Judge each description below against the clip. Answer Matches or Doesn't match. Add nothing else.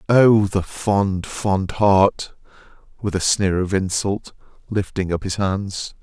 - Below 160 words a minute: Matches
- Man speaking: Matches